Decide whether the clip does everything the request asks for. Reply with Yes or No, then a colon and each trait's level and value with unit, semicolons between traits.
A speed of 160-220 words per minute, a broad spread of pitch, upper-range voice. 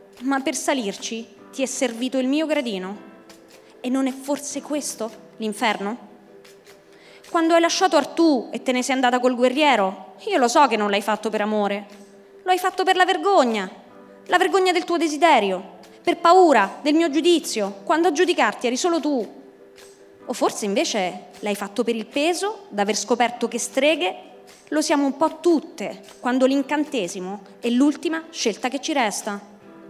Yes: average, 165 wpm; wide, 7.3 semitones; very high, 260 Hz